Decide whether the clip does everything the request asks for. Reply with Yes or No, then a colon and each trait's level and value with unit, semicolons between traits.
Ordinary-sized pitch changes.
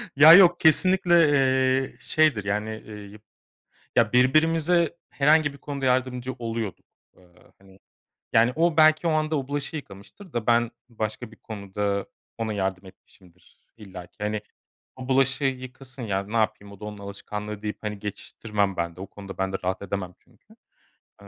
No: wide, 5.7 semitones